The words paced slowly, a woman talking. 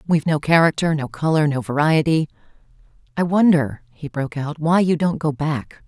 No: average, 165 wpm; female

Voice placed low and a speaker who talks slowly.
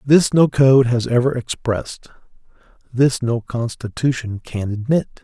Yes: low, 125 Hz; slow, 125 wpm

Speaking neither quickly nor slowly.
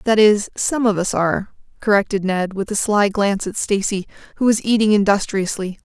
Yes: average, 185 wpm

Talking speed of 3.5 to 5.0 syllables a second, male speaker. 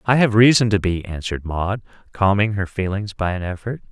No: 5.6 syllables/s; male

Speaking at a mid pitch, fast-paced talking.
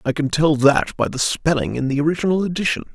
Yes: medium, 150 Hz; fast, 225 wpm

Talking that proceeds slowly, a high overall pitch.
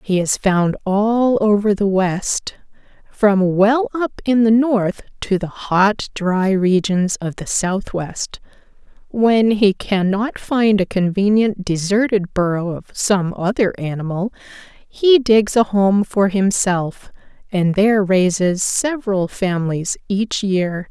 Yes: slow, 130 wpm; high, 200 Hz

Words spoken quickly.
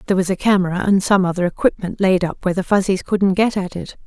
Yes: fast, 250 wpm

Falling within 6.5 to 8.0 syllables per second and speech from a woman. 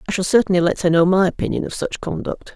Yes: 6.8 syllables/s; female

